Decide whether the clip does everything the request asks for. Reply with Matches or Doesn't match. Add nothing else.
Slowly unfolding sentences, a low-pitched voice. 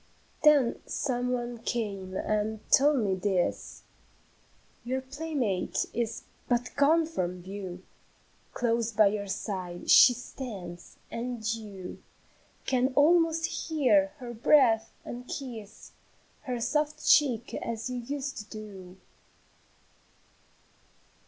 Doesn't match